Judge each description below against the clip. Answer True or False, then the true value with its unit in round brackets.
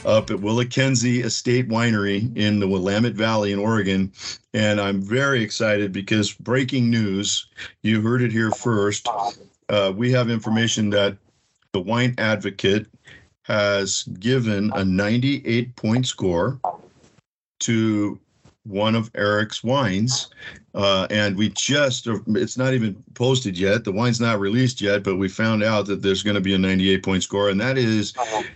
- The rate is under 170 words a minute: True (155 wpm)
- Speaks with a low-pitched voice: True (110 Hz)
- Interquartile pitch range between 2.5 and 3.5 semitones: True (3.0 semitones)